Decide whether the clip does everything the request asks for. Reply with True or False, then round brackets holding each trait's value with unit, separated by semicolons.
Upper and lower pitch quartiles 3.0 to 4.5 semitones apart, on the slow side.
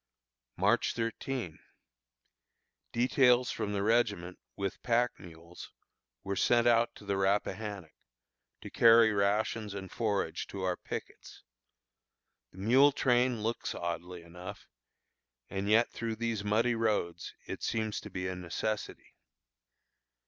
True (3.6 semitones; 120 wpm)